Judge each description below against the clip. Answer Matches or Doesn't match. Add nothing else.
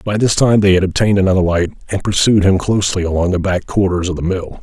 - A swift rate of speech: Matches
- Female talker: Doesn't match